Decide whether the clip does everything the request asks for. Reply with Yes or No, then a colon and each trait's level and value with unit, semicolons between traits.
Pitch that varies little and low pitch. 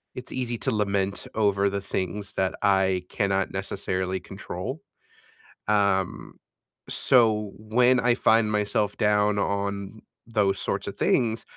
Yes: narrow, 2.1 semitones; low, 100 Hz